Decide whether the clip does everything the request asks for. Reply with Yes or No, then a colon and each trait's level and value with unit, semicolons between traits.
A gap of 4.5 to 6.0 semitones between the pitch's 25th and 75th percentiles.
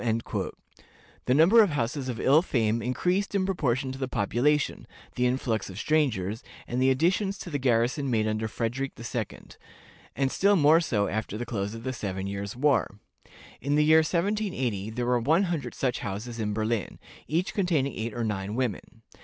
Yes: average, 5.3 semitones